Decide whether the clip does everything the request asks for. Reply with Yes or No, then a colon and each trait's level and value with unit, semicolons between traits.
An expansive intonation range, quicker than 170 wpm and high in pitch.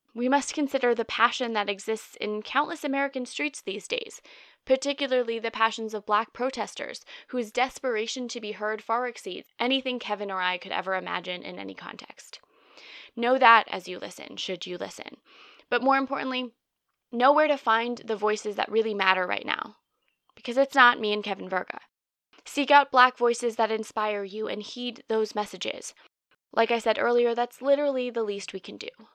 No: average, 3.6 semitones; average, 180 wpm; high, 240 Hz